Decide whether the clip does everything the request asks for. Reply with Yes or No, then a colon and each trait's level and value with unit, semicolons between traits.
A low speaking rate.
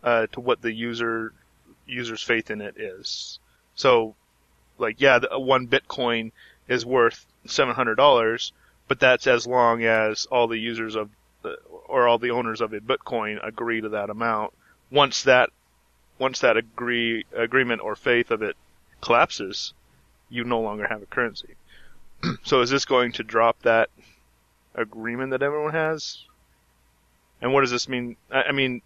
No: average, 160 wpm